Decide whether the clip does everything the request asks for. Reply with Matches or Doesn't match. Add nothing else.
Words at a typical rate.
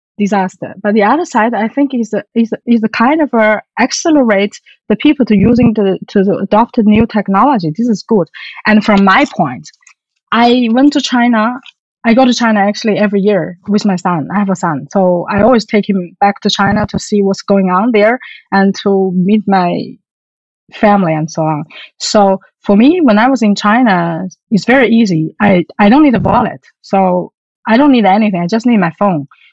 Doesn't match